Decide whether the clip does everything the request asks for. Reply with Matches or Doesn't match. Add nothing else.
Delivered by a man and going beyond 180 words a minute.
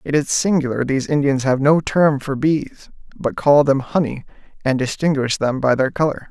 Matches